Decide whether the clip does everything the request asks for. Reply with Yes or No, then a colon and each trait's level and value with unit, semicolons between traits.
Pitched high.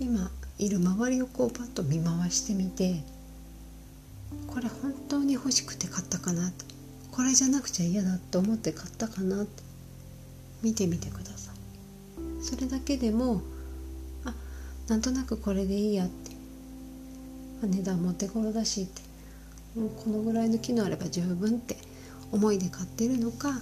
Yes: high, 195 Hz